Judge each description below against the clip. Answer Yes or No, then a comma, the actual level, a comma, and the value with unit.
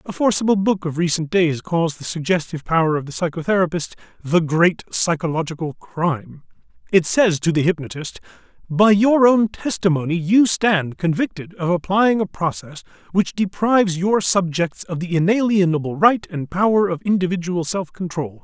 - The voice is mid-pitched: Yes, medium, 175 Hz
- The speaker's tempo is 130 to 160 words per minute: Yes, average, 155 wpm